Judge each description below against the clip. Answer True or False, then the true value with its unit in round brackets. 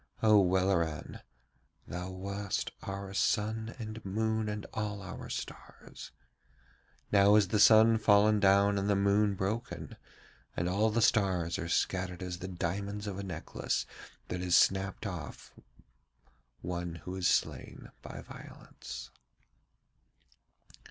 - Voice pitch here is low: True (100 Hz)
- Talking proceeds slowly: True (125 wpm)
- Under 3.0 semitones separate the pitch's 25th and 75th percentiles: True (2.5 semitones)